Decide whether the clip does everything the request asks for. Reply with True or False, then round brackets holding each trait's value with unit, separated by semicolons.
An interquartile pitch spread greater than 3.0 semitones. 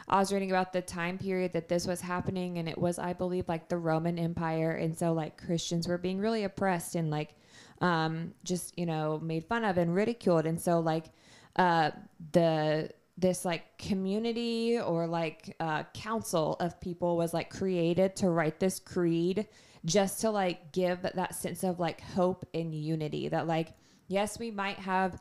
False (2.5 semitones)